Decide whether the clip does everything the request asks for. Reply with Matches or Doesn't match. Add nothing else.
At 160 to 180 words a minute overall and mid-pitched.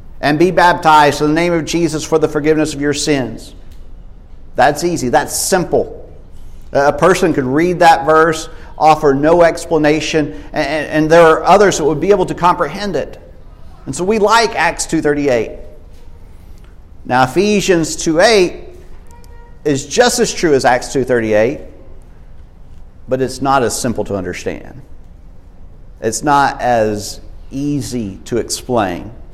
Doesn't match